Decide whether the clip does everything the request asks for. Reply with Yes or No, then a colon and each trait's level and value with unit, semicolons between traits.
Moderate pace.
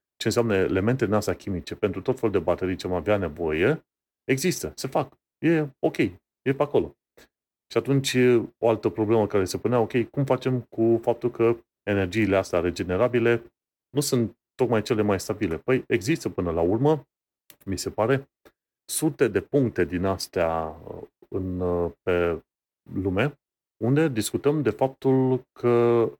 Yes: average, 150 wpm